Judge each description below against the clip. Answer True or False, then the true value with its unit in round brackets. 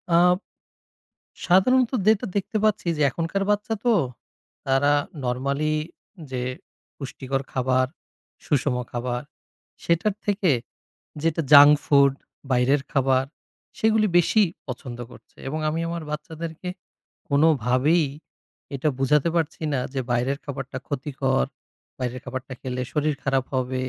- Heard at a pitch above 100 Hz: True (140 Hz)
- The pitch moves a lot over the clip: False (4.2 semitones)